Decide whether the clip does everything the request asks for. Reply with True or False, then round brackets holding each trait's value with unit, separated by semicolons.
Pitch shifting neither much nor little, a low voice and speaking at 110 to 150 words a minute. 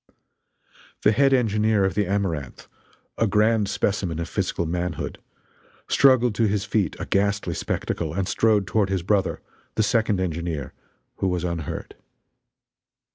True (3.2 semitones; 100 Hz; 135 wpm)